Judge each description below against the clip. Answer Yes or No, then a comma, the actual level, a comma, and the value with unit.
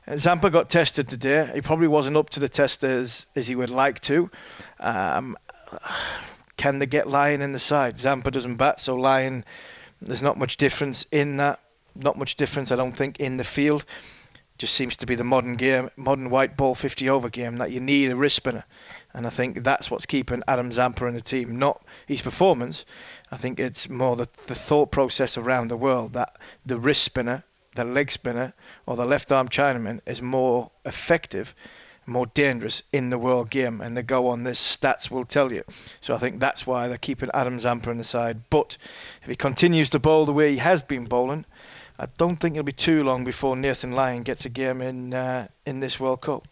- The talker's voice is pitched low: Yes, low, 130 Hz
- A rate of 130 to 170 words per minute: No, fast, 205 wpm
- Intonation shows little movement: Yes, narrow, 2.2 semitones